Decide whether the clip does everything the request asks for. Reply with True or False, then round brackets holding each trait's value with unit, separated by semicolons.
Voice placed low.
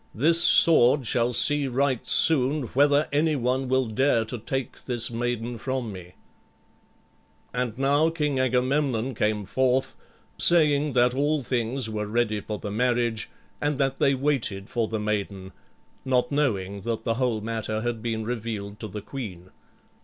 True (125 Hz)